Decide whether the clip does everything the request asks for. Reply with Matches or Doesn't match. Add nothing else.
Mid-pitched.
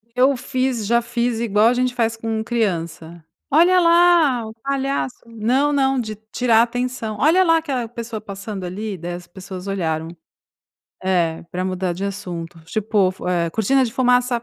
Doesn't match